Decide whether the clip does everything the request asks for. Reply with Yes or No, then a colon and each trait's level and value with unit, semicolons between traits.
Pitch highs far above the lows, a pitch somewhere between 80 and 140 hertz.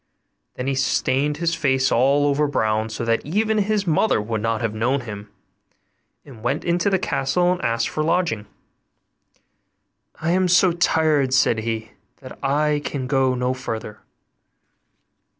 Yes: wide, 5.9 semitones; low, 135 Hz